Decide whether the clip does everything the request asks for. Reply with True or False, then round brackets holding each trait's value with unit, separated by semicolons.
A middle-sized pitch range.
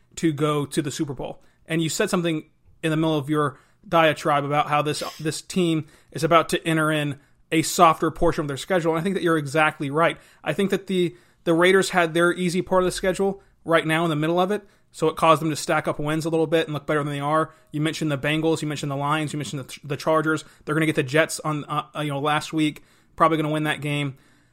False (1.8 semitones)